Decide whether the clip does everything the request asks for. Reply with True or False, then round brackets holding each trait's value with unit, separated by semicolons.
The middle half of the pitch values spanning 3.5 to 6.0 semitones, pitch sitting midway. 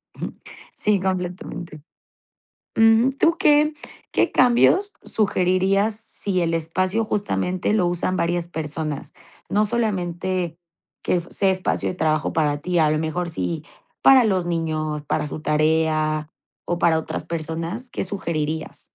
True (4.1 semitones; 175 Hz)